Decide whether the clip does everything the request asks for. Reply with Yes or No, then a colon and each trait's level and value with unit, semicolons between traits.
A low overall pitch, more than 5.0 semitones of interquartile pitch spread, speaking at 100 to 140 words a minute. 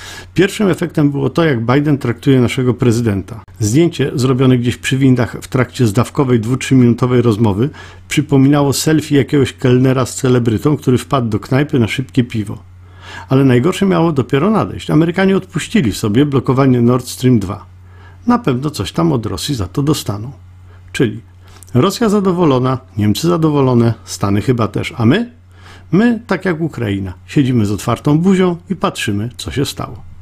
No: low, 125 Hz; wide, 5.5 semitones; average, 150 wpm